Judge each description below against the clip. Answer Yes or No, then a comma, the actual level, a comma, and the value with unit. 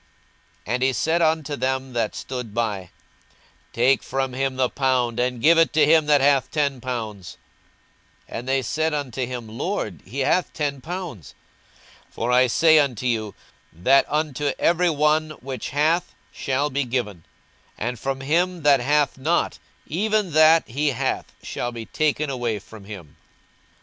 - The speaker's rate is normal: Yes, average, 165 wpm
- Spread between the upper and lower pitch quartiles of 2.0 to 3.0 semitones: No, average, 4.0 semitones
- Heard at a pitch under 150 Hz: Yes, low, 135 Hz